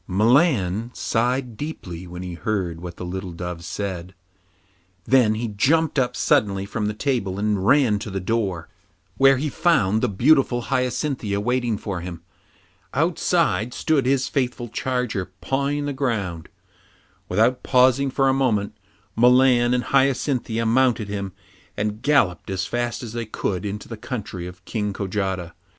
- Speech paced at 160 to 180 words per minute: No, average, 150 wpm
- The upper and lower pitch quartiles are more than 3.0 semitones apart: Yes, average, 5.0 semitones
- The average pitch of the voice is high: No, low, 110 Hz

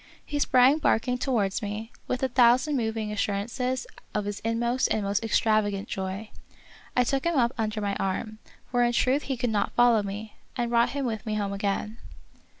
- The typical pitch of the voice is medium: No, high, 225 Hz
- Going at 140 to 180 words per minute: No, average, 190 wpm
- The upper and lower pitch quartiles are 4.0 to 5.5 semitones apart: No, average, 3.1 semitones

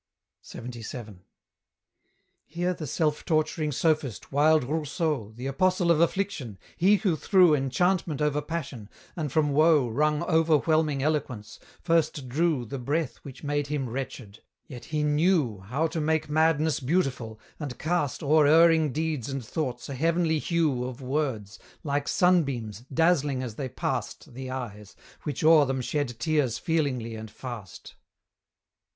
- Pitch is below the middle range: No, medium, 150 Hz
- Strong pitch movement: No, average, 4.0 semitones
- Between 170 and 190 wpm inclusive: No, average, 140 wpm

